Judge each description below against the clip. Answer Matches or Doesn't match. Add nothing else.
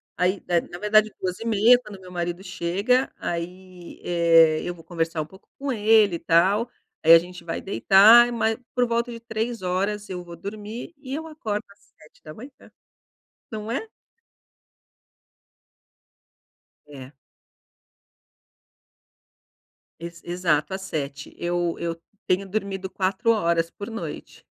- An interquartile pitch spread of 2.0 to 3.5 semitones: Doesn't match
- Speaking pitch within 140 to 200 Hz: Matches